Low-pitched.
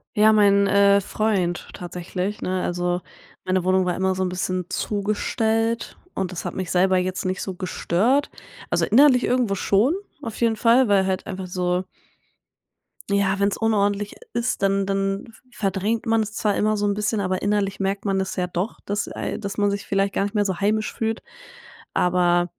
No: high, 200 Hz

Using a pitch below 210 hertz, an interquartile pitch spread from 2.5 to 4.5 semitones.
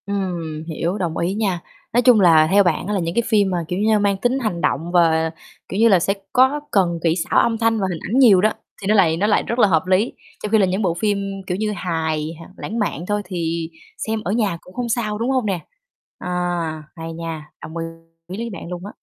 Yes: high, 190 Hz; average, 4.1 semitones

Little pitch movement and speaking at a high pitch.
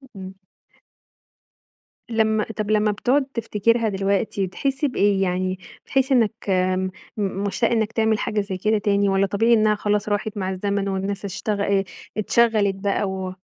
Yes: narrow, 2.2 semitones; high, 205 Hz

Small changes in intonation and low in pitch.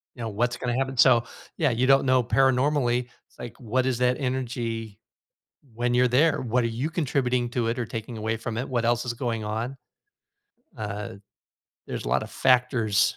Yes: narrow, 2.0 semitones; low, 120 Hz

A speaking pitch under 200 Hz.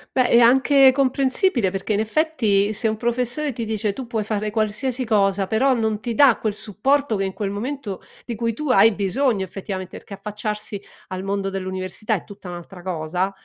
No: high, 215 Hz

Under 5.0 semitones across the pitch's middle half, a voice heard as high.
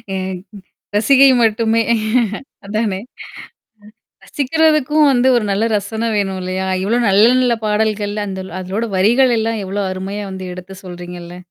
Yes: average, 3.6 semitones; high, 210 Hz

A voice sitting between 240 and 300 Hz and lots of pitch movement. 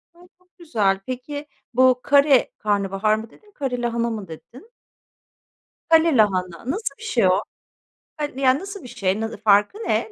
Yes: high, 245 Hz; wide, 6.3 semitones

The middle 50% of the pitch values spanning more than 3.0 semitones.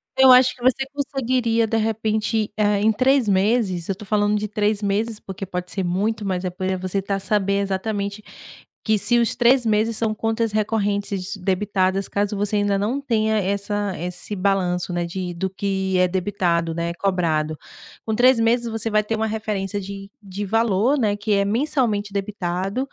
No: narrow, 2.6 semitones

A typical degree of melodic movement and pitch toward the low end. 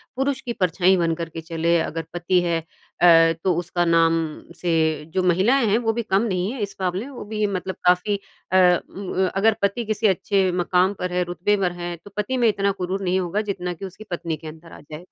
No: average, 3.0 semitones; medium, 185 Hz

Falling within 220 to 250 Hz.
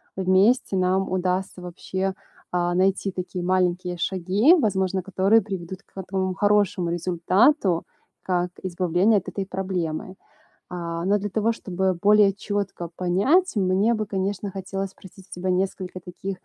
No: high, 190 Hz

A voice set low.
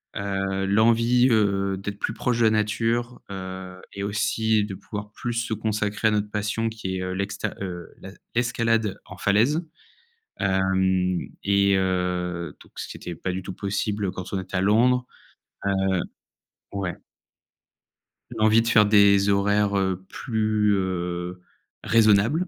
Yes: low, 100 Hz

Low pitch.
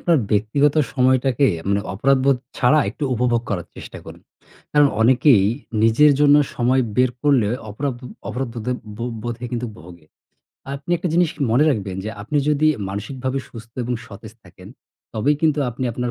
Yes: low, 125 Hz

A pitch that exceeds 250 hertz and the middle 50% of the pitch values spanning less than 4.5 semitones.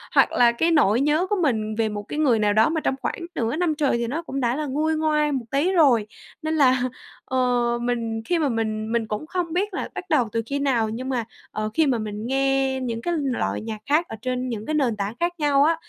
No: very high, 260 Hz; average, 5.1 semitones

